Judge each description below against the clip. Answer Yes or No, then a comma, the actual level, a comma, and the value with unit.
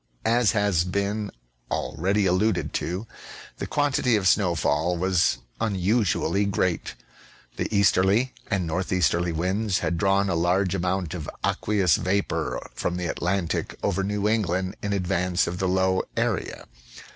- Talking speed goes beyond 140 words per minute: No, slow, 135 wpm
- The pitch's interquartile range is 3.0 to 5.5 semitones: No, narrow, 2.4 semitones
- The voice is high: No, very low, 95 Hz